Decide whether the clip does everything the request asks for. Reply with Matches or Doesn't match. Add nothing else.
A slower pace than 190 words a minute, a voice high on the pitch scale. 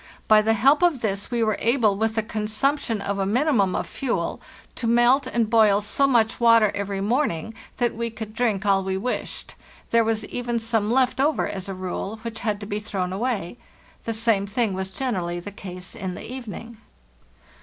Doesn't match